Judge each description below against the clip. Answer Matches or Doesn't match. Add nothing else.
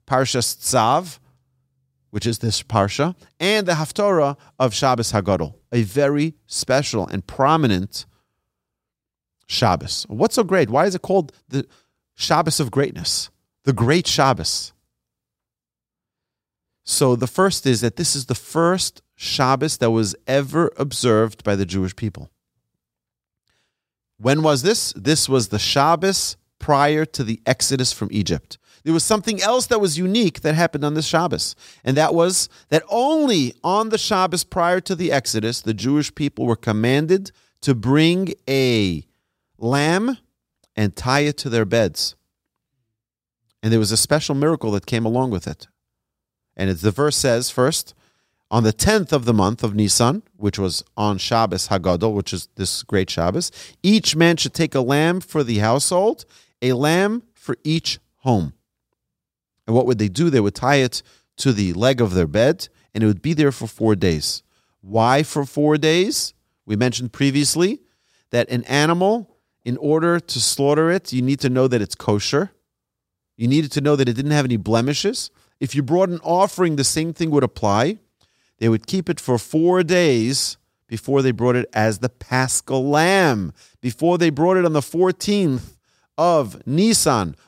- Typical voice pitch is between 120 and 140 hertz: Matches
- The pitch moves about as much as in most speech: Doesn't match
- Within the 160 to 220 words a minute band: Matches